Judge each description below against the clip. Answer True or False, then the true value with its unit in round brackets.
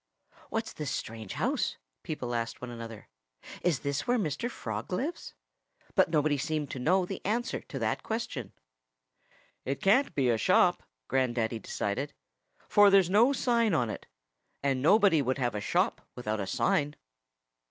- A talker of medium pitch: True (145 Hz)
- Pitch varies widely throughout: True (8.5 semitones)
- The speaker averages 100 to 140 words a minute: False (155 wpm)